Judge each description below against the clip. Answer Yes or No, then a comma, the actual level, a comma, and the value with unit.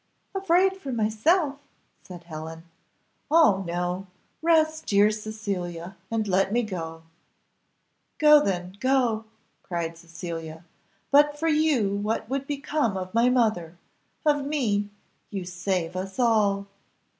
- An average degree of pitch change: No, wide, 7.6 semitones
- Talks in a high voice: Yes, high, 210 Hz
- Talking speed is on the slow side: Yes, slow, 120 wpm